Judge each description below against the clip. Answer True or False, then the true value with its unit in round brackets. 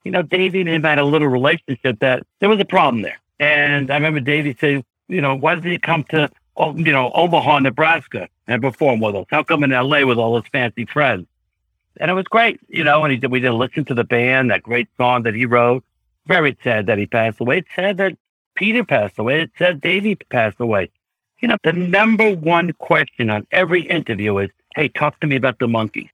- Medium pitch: True (145 Hz)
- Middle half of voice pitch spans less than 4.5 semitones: False (5.4 semitones)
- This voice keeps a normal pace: False (225 wpm)